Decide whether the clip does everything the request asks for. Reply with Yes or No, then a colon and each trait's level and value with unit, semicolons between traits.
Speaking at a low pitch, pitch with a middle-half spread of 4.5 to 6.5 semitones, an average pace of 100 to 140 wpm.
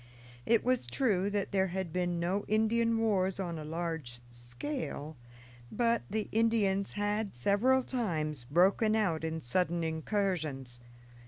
No: high, 190 Hz; average, 5.2 semitones; slow, 135 wpm